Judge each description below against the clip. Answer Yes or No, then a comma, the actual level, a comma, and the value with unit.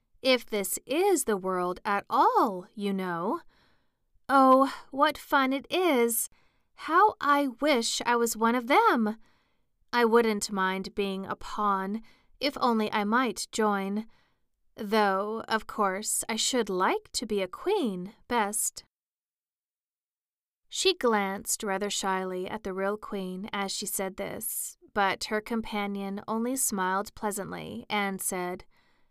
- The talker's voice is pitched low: No, high, 215 Hz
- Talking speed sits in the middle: No, slow, 130 wpm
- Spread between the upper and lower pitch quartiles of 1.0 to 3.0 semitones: No, average, 4.2 semitones